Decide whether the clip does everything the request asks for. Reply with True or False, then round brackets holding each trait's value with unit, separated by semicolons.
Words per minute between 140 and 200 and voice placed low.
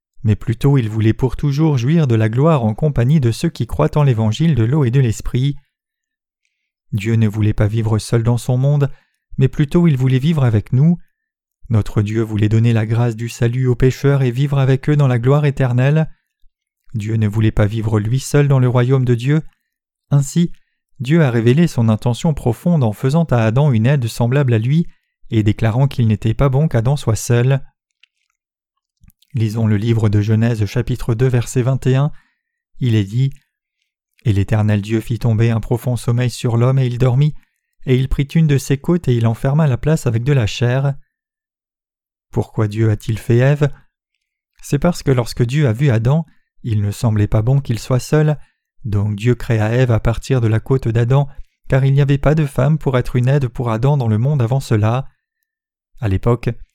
True (195 wpm; 125 Hz)